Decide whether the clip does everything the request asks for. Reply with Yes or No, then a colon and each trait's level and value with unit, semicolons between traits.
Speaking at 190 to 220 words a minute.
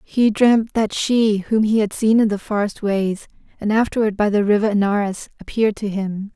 Yes: average, 200 wpm